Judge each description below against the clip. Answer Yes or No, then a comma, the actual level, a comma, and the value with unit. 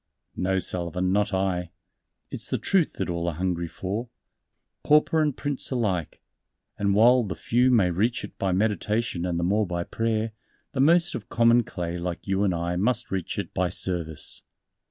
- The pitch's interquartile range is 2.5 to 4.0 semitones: No, average, 4.8 semitones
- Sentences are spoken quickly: No, average, 175 wpm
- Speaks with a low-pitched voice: Yes, very low, 95 Hz